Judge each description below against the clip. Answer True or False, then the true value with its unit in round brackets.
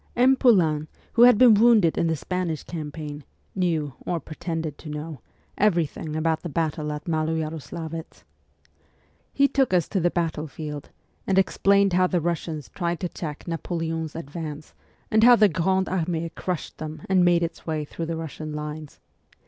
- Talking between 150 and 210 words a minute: True (165 wpm)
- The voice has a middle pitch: True (165 Hz)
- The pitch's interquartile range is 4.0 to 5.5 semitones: False (2.9 semitones)